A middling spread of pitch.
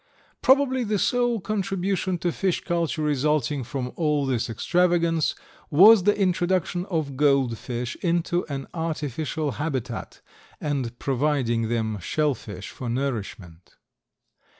No: wide, 5.8 semitones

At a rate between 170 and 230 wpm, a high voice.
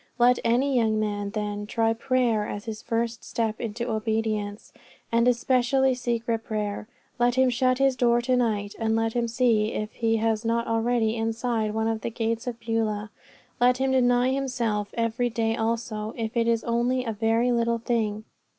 Yes: average, 180 wpm; high, 230 Hz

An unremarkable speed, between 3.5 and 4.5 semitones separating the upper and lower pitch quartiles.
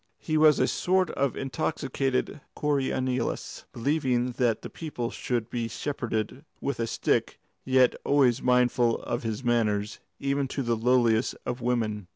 No: average, 145 wpm; average, 2.8 semitones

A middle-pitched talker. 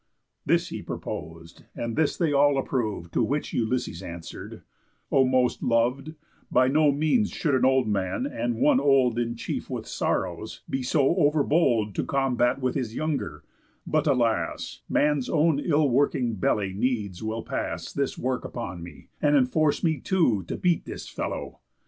No: low, 130 Hz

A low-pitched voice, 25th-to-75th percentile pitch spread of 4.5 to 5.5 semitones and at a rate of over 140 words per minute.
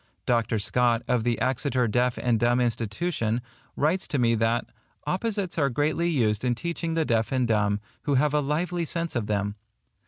Yes: low, 125 Hz; average, 5.1 semitones; average, 180 wpm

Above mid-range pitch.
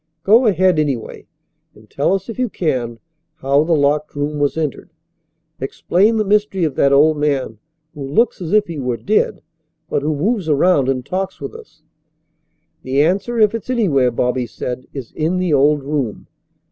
No: medium, 150 Hz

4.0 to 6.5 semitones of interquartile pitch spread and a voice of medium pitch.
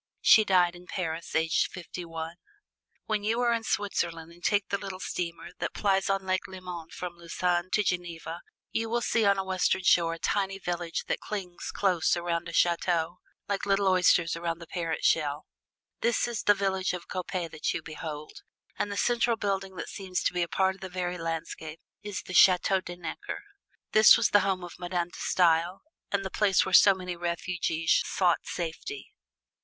No: narrow, 2.5 semitones; medium, 180 Hz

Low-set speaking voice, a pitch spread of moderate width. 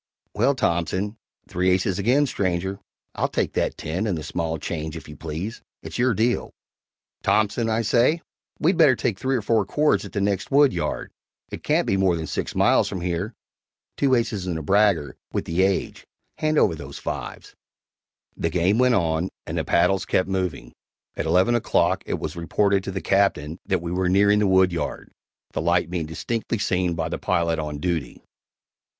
Yes: very low, 95 Hz; average, 4.1 semitones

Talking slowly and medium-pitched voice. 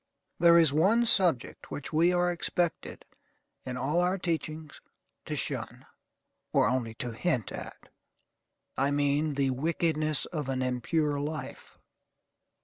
Yes: slow, 130 wpm; medium, 155 Hz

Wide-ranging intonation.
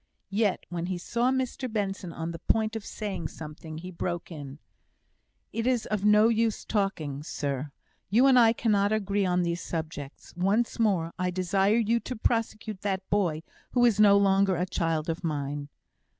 No: average, 4.7 semitones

